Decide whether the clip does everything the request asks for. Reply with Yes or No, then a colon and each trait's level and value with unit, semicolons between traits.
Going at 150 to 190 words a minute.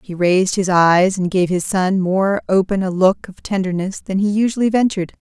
No: fast, 205 wpm